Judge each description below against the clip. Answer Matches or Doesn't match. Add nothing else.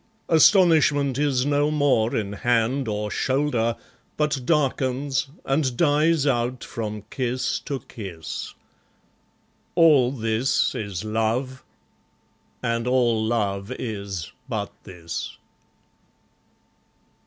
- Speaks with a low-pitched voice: Matches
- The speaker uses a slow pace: Matches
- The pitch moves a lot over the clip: Doesn't match